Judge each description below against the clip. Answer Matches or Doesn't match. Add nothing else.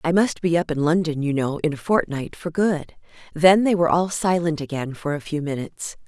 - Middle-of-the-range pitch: Matches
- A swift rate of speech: Matches